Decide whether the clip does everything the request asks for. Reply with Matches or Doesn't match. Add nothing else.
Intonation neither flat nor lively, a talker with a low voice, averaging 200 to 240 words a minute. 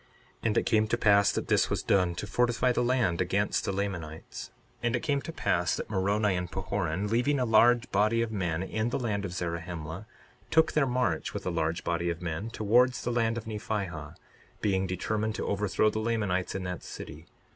Matches